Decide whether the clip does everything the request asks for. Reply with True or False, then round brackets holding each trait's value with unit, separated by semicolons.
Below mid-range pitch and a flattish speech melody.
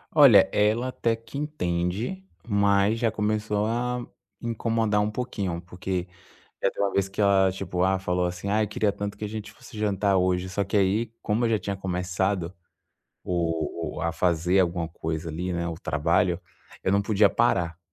False (100 Hz; 3.1 semitones)